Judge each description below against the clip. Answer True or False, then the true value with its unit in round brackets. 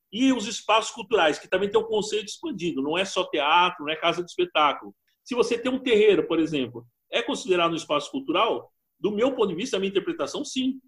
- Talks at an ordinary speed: False (225 wpm)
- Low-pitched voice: False (210 Hz)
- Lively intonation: True (6.9 semitones)